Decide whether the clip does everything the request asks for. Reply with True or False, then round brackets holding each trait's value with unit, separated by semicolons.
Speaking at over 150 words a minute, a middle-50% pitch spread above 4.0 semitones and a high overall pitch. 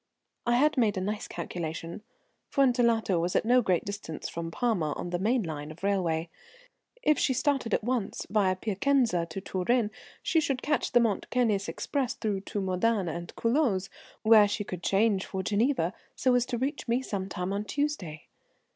True (180 wpm; 5.1 semitones; 210 Hz)